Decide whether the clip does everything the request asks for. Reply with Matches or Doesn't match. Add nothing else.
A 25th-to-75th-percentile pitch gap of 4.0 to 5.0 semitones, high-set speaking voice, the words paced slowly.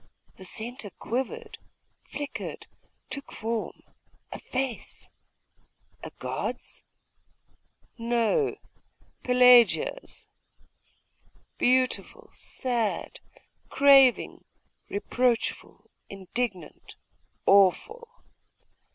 Doesn't match